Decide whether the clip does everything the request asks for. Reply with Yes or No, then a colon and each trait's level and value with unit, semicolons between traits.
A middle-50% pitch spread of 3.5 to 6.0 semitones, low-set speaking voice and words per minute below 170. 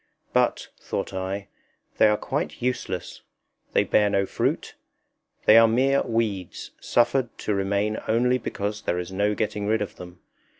No: average, 2.7 semitones; low, 105 Hz; average, 155 wpm